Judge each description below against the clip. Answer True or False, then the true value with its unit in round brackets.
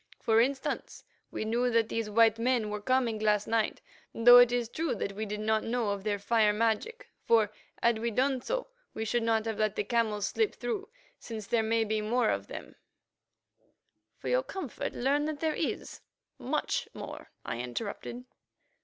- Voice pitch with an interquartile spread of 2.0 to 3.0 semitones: True (2.5 semitones)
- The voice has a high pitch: True (230 Hz)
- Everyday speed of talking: True (185 wpm)